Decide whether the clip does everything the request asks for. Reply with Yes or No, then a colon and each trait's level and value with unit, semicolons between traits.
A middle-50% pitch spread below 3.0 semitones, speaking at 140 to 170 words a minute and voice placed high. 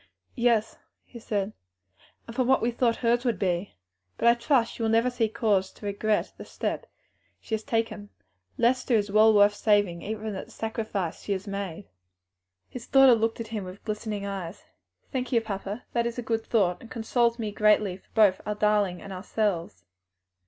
No: narrow, 2.6 semitones; average, 185 wpm; high, 215 Hz